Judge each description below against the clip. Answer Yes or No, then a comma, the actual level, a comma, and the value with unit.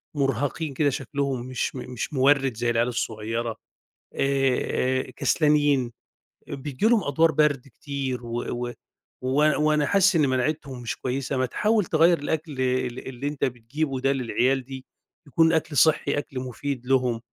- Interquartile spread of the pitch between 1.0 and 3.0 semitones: Yes, average, 2.7 semitones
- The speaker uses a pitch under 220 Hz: Yes, low, 135 Hz